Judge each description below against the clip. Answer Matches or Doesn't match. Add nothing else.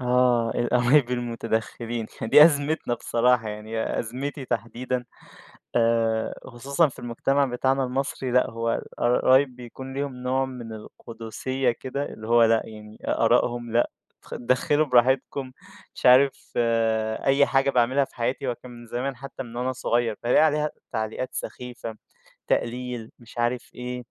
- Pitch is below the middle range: Matches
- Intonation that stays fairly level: Matches